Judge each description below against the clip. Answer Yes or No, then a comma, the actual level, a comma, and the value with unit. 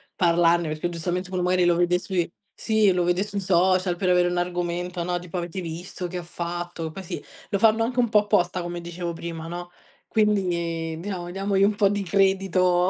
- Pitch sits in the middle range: Yes, medium, 180 Hz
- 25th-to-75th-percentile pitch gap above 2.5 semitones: No, narrow, 1.9 semitones